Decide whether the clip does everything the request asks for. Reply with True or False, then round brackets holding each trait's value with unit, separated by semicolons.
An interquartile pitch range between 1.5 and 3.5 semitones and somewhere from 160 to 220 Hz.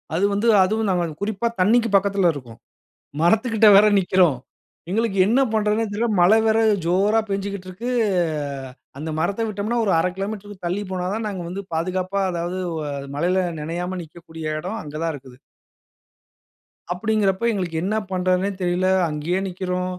True (3.0 semitones; 185 Hz)